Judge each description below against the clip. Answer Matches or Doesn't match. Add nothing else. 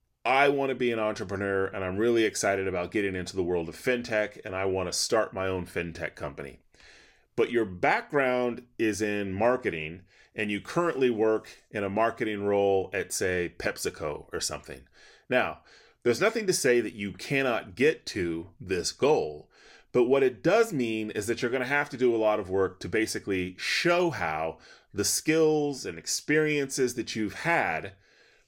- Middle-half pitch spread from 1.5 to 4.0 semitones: Doesn't match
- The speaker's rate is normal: Matches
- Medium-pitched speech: Doesn't match